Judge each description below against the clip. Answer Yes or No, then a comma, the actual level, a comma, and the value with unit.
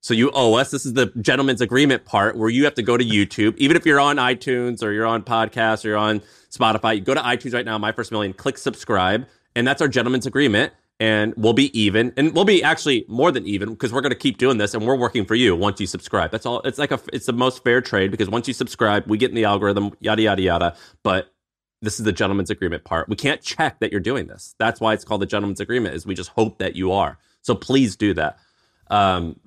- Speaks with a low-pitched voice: Yes, low, 115 Hz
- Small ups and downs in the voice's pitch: No, average, 3.5 semitones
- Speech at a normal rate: No, fast, 260 wpm